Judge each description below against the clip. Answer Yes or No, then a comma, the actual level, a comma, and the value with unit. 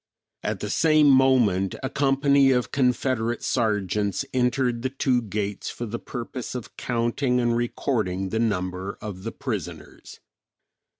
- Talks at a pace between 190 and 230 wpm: No, slow, 135 wpm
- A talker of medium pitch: No, low, 120 Hz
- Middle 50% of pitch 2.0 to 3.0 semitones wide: No, average, 4.1 semitones